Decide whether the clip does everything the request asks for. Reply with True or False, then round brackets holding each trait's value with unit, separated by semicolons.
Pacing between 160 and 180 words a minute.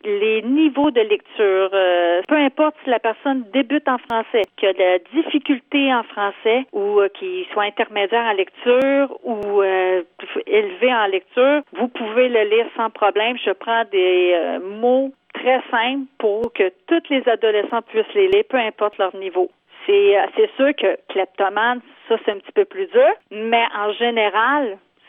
True (175 wpm)